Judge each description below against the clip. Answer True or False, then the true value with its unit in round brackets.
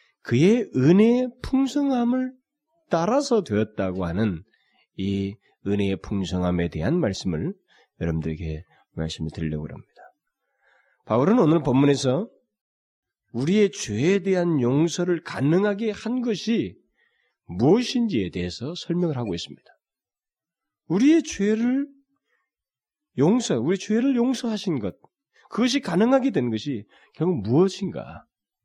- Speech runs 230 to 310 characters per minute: True (255 characters per minute)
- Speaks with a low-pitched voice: False (180 Hz)